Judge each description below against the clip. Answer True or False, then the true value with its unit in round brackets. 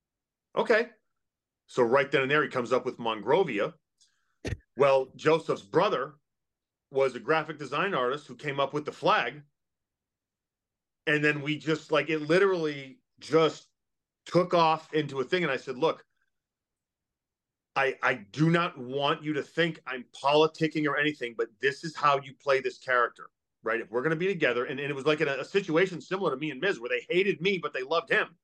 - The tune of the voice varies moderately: True (3.2 semitones)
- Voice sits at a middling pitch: True (150 Hz)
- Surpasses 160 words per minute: True (190 wpm)